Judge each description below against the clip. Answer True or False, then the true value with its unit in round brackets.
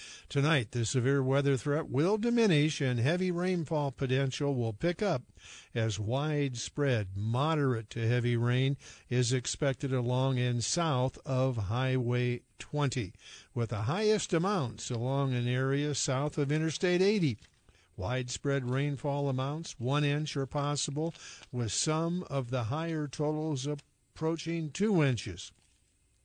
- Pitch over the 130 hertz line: True (140 Hz)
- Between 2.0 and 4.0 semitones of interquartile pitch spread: True (3.7 semitones)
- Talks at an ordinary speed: False (125 wpm)